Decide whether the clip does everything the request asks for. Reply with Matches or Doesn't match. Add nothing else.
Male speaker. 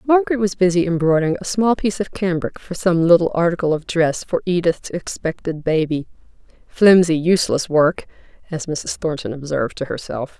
Doesn't match